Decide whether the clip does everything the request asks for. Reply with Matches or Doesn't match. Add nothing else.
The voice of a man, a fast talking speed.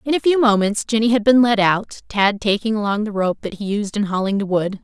Doesn't match